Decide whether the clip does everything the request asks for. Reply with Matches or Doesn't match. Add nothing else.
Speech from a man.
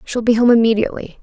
Doesn't match